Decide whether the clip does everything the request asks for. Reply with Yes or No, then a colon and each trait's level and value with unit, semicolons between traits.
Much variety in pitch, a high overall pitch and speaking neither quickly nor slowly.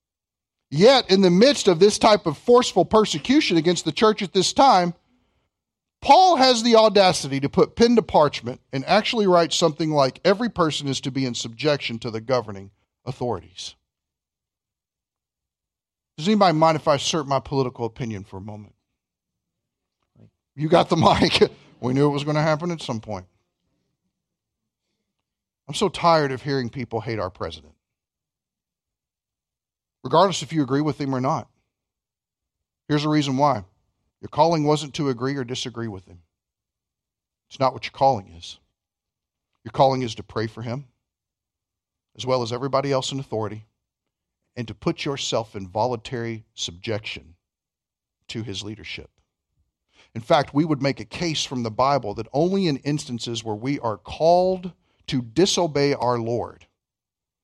No: wide, 6.7 semitones; low, 135 Hz; average, 155 wpm